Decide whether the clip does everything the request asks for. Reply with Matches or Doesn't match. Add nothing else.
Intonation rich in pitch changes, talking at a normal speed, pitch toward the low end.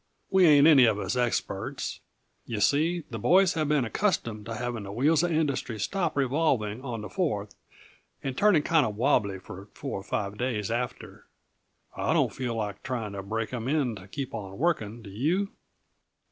Matches